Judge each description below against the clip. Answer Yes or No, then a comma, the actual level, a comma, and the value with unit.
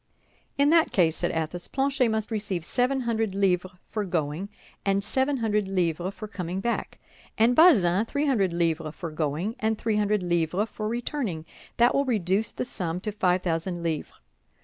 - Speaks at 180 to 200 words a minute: No, average, 170 wpm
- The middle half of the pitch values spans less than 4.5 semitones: No, average, 4.8 semitones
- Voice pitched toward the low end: No, high, 200 Hz